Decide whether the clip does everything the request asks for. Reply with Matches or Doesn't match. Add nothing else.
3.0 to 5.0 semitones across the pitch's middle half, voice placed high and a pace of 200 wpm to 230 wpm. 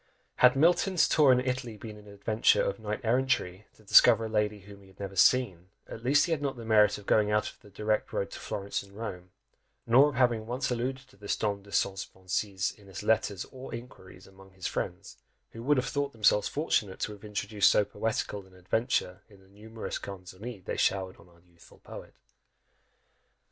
Doesn't match